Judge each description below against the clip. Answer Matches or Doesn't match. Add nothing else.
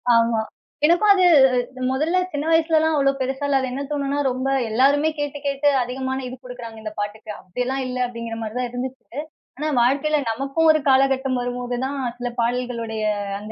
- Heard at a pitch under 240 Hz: Doesn't match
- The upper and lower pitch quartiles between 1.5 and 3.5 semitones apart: Matches